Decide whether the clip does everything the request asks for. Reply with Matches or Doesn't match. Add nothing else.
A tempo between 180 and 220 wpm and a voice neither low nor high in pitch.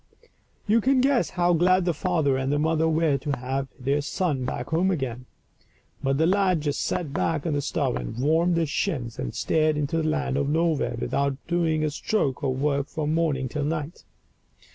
Matches